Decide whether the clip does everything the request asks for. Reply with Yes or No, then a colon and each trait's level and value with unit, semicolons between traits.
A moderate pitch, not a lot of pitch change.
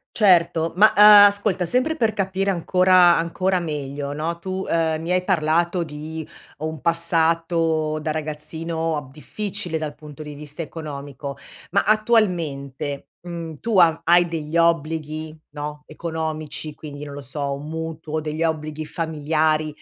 Yes: medium, 160 Hz; narrow, 2.2 semitones